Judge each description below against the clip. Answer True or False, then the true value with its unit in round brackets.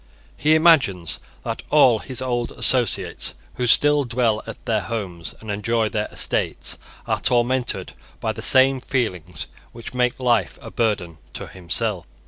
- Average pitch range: True (3.7 semitones)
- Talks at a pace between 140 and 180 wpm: True (145 wpm)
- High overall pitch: False (115 Hz)